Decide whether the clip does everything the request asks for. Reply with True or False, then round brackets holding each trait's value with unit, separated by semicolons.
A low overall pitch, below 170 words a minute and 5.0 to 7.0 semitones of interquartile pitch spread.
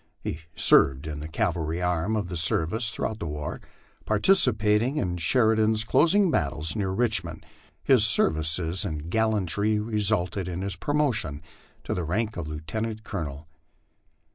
True (95 Hz; 150 wpm; 5.3 semitones)